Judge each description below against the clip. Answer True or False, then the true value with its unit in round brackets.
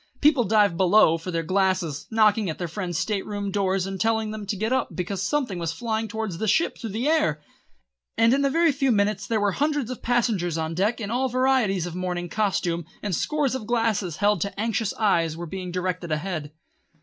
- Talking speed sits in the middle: False (215 wpm)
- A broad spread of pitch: False (4.1 semitones)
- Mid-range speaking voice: False (205 Hz)